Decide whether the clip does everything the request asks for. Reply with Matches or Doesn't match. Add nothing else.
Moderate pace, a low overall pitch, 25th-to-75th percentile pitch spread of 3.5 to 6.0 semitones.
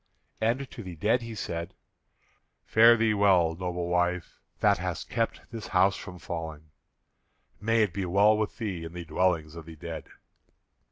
Matches